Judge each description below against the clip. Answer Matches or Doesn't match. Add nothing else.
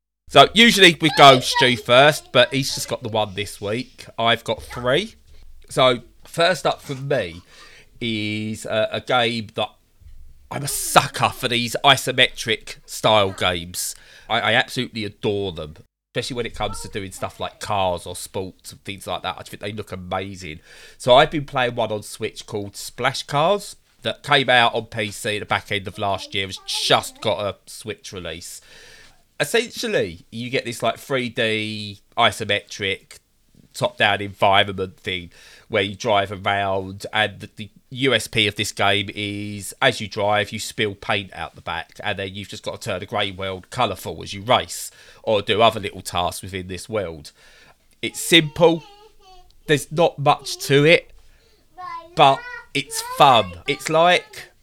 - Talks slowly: Doesn't match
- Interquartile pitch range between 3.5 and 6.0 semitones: Matches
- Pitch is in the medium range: Doesn't match